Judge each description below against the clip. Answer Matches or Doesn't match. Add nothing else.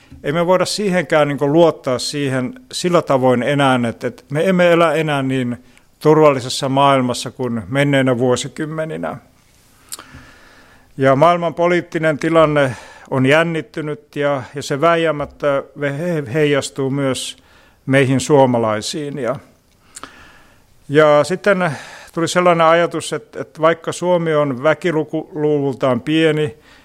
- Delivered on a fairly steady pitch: Doesn't match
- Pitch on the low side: Doesn't match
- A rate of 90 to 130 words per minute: Matches